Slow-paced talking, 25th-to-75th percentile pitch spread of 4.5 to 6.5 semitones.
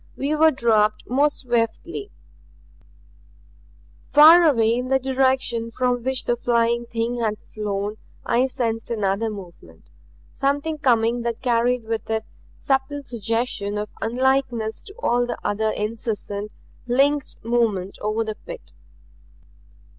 No: slow, 125 wpm; average, 3.1 semitones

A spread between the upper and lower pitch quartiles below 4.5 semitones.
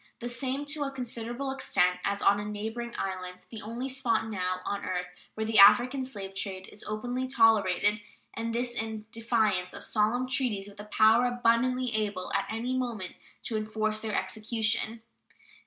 Yes: average, 2.9 semitones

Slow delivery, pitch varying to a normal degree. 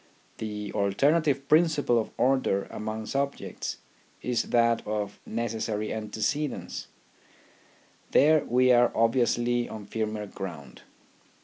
Yes: slow, 105 wpm; average, 3.6 semitones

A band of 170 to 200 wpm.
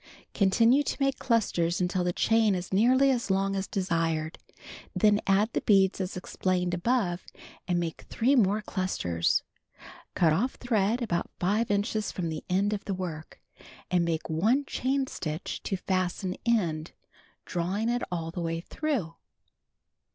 No: average, 155 wpm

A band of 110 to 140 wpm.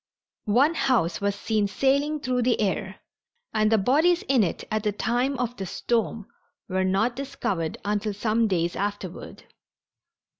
No: average, 150 wpm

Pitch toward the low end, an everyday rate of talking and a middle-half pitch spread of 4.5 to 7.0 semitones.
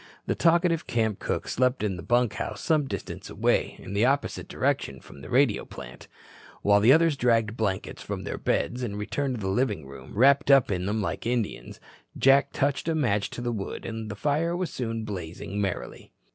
Yes: low, 115 Hz; average, 195 wpm; average, 5.1 semitones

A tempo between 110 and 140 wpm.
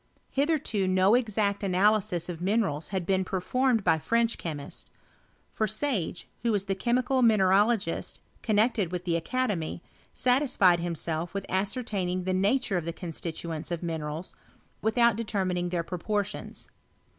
Yes: slow, 135 wpm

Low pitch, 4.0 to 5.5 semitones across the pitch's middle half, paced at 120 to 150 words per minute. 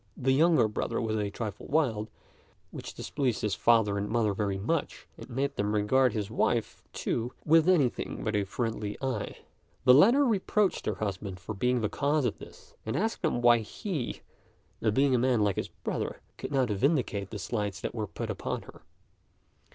No: low, 115 Hz; average, 4.8 semitones; average, 180 wpm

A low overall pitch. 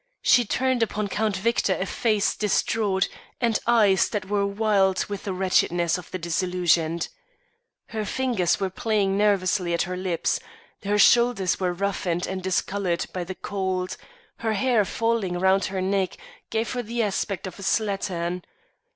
No: high, 195 Hz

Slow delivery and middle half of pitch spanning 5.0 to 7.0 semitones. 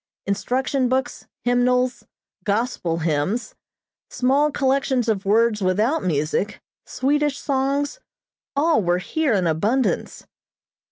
Yes: slow, 100 wpm; average, 5.3 semitones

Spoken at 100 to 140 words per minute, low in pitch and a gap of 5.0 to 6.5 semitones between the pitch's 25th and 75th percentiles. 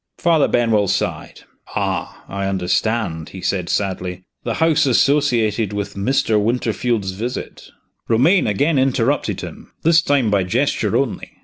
Yes: slow, 135 wpm; low, 115 Hz; wide, 5.4 semitones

